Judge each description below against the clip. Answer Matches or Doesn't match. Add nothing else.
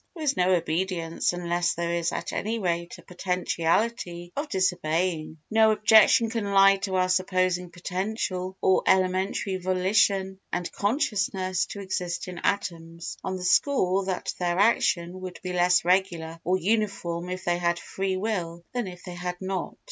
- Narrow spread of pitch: Matches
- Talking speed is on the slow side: Doesn't match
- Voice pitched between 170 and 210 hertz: Matches